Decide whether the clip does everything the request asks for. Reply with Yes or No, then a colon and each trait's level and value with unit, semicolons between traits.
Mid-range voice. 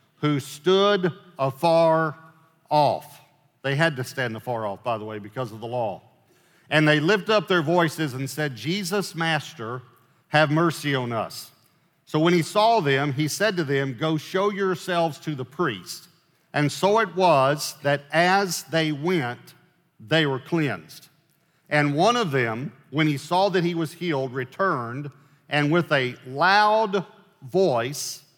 Yes: medium, 155 Hz